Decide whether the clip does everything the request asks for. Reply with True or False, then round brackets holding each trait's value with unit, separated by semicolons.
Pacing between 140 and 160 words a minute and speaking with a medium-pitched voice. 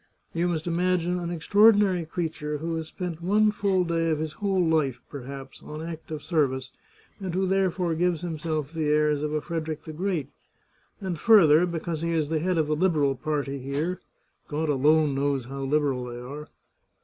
False (180 wpm; 160 Hz)